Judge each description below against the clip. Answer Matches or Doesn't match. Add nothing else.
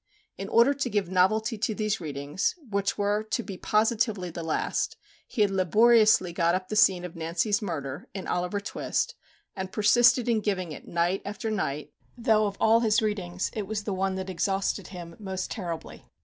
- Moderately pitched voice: Doesn't match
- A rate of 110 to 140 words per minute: Doesn't match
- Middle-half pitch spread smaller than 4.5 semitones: Matches